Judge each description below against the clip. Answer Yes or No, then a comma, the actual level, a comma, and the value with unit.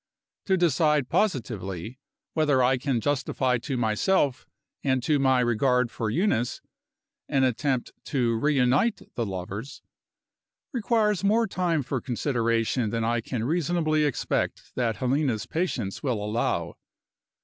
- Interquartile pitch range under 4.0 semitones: No, average, 4.6 semitones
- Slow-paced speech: Yes, slow, 125 wpm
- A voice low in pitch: Yes, low, 130 Hz